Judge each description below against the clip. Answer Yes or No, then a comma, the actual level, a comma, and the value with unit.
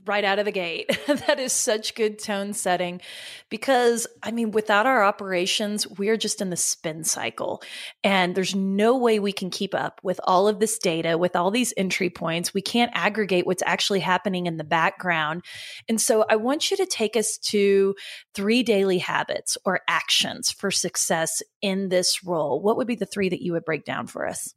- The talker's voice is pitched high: Yes, high, 200 Hz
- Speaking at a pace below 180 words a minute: No, average, 200 wpm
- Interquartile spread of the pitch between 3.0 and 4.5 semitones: Yes, average, 3.3 semitones